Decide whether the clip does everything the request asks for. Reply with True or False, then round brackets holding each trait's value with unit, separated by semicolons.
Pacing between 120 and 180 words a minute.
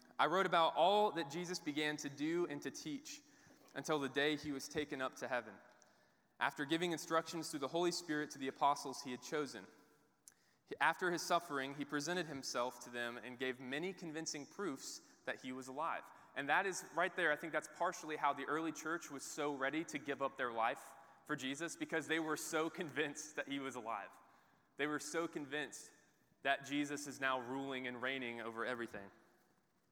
False (195 wpm)